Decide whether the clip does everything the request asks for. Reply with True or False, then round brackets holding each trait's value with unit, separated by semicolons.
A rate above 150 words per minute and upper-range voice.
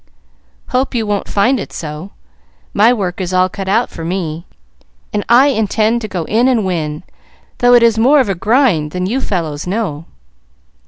True (180 wpm; 205 Hz)